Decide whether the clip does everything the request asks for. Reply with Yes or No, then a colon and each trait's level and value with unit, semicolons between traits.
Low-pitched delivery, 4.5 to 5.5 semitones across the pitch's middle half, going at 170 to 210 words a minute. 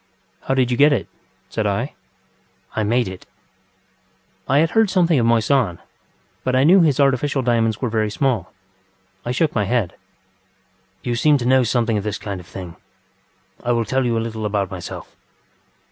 No: low, 120 Hz; average, 3.9 semitones; average, 175 wpm